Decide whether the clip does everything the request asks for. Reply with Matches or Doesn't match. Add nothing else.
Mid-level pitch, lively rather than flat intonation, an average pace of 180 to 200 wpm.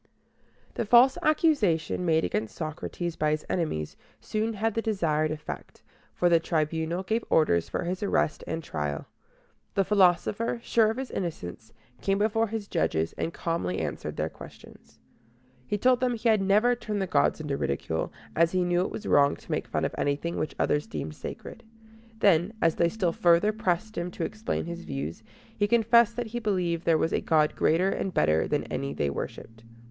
Matches